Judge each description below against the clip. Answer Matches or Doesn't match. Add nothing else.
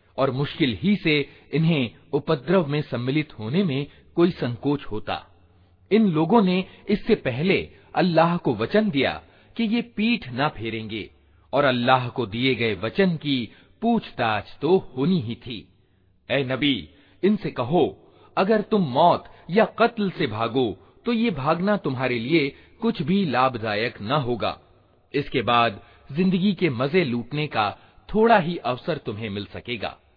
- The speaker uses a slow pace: Doesn't match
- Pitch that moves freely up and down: Matches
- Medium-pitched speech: Matches